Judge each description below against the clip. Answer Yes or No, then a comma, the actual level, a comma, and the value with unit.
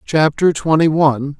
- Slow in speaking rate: Yes, slow, 130 wpm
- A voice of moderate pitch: Yes, medium, 155 Hz